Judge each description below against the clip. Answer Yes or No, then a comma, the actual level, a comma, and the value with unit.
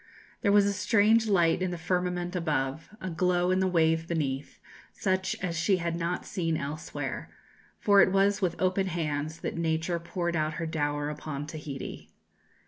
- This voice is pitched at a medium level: Yes, medium, 170 Hz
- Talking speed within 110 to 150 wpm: No, average, 170 wpm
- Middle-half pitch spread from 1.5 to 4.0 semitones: Yes, average, 2.8 semitones